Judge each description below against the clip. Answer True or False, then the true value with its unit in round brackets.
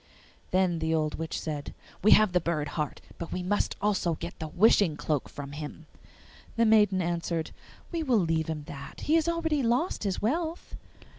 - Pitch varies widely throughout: True (5.7 semitones)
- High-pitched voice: False (175 Hz)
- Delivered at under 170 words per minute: False (180 wpm)